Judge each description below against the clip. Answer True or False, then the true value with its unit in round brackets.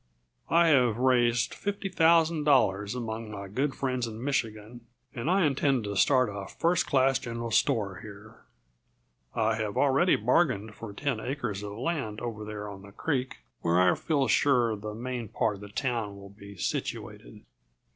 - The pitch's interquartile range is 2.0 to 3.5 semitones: False (4.6 semitones)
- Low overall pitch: True (115 Hz)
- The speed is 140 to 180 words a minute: True (165 wpm)